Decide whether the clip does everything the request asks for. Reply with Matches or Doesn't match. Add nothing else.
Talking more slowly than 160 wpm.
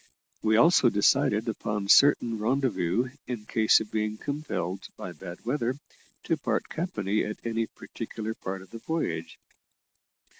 Matches